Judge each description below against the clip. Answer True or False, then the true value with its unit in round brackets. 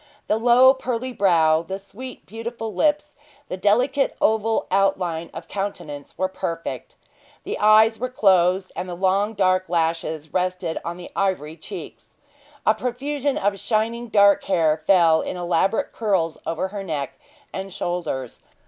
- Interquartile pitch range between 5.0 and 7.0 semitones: False (4.5 semitones)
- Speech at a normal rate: True (145 wpm)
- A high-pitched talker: True (195 Hz)